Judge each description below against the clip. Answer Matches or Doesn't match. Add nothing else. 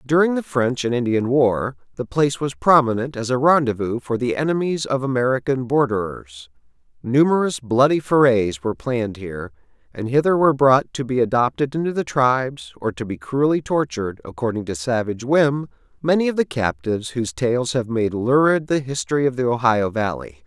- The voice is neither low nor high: Doesn't match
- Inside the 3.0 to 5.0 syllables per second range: Doesn't match